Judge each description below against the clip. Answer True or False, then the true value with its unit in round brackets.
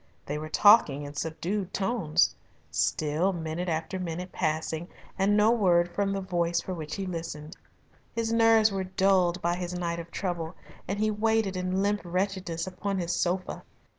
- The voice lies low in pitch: False (180 Hz)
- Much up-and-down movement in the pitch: False (2.9 semitones)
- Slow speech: False (165 wpm)